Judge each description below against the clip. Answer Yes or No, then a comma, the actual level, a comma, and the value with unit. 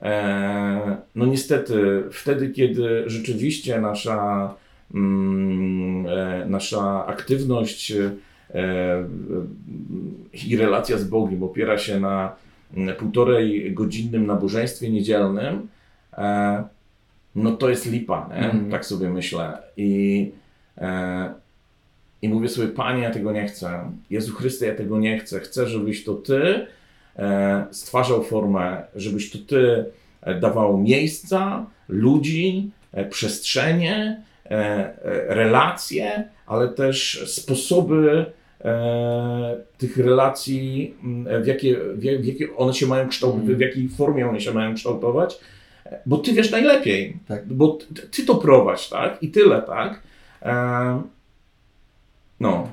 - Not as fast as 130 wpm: Yes, slow, 110 wpm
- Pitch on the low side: Yes, low, 110 Hz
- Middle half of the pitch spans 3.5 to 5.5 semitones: Yes, average, 4.7 semitones